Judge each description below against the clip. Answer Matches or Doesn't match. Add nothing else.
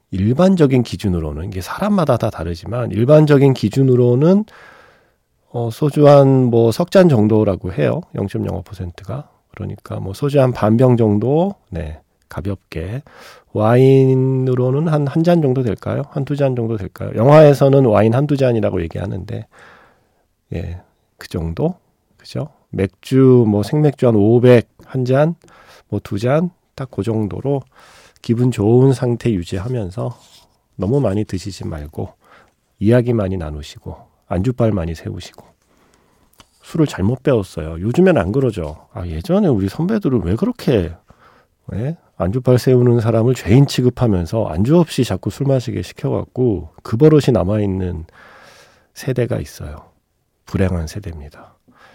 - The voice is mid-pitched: Doesn't match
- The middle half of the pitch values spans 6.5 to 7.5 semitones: Doesn't match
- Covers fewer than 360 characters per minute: Matches